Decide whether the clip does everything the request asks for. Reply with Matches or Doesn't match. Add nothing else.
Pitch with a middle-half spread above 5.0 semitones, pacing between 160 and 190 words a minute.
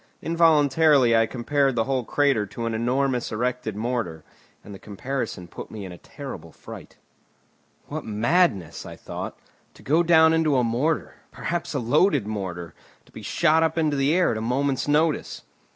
Matches